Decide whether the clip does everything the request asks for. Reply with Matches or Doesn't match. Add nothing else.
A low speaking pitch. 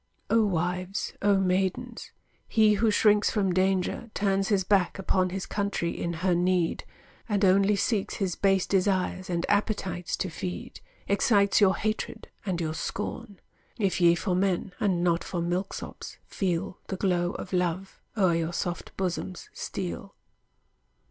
Doesn't match